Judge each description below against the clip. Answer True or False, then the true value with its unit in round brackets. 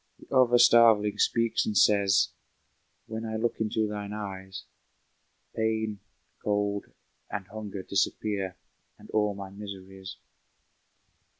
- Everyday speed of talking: False (110 wpm)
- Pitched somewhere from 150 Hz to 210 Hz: False (105 Hz)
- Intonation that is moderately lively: False (2.0 semitones)